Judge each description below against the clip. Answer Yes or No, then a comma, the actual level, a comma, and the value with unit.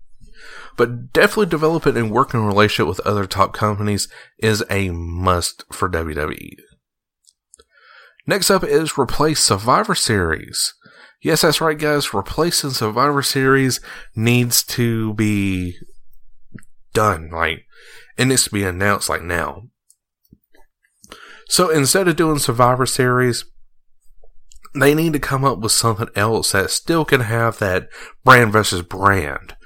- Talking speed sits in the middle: No, slow, 125 wpm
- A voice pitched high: No, low, 115 Hz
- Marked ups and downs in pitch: Yes, wide, 5.8 semitones